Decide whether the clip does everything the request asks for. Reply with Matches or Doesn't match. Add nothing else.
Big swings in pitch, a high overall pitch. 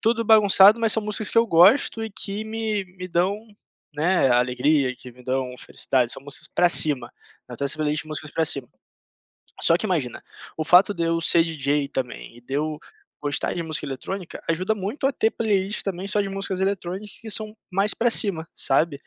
Doesn't match